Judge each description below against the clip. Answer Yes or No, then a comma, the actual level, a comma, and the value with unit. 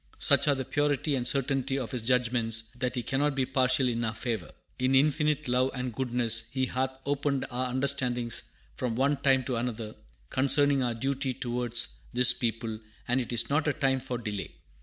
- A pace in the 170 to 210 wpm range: Yes, average, 185 wpm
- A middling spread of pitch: No, narrow, 2.2 semitones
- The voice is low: Yes, low, 125 Hz